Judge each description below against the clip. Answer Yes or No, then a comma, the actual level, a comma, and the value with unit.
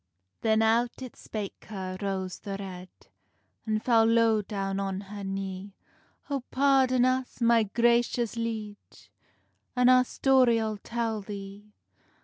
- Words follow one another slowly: Yes, slow, 130 wpm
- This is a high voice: Yes, high, 220 Hz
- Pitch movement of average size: Yes, average, 3.3 semitones